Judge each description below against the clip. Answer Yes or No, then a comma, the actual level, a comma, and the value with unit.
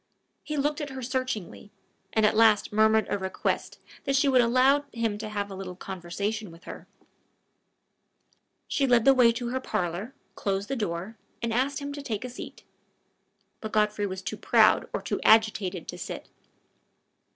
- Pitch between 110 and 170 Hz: No, high, 220 Hz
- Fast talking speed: No, average, 175 wpm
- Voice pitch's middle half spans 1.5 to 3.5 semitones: No, average, 4.2 semitones